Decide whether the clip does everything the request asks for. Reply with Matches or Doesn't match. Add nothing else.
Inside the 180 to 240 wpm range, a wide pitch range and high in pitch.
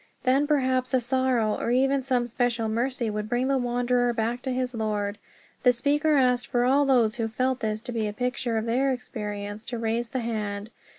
Doesn't match